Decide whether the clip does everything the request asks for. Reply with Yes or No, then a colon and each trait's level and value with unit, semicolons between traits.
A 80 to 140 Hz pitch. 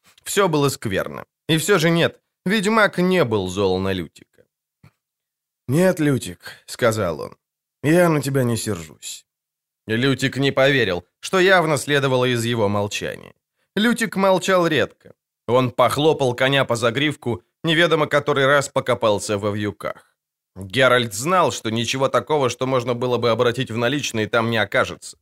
Yes: low, 135 Hz